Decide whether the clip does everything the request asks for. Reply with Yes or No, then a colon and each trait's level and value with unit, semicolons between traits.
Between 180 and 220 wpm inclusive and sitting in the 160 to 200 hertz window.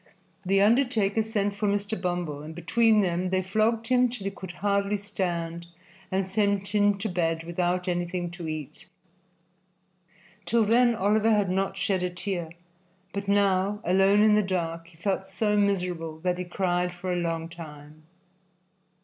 No: average, 160 wpm; high, 190 Hz